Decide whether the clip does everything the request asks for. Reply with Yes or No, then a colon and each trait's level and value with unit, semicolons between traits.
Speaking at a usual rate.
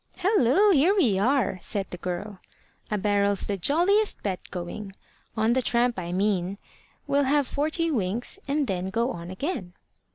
Yes: average, 160 wpm